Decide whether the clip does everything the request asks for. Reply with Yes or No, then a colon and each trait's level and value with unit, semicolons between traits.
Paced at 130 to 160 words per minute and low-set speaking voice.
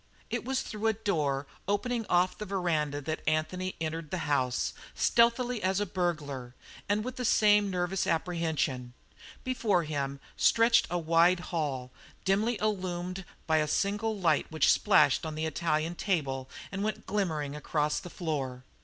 No: average, 155 wpm; medium, 175 Hz